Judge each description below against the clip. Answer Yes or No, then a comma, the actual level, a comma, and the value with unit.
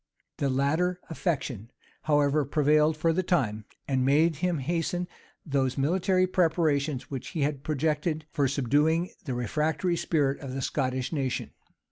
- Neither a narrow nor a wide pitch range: Yes, average, 3.4 semitones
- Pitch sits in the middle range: Yes, medium, 150 Hz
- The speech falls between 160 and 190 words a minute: No, average, 140 wpm